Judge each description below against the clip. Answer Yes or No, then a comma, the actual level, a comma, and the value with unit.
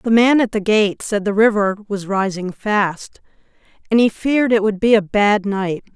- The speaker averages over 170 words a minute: Yes, average, 200 wpm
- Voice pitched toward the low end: No, high, 210 Hz